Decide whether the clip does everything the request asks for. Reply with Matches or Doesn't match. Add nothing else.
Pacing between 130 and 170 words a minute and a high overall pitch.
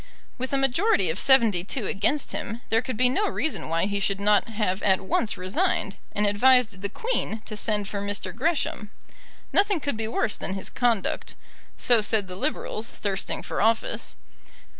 Doesn't match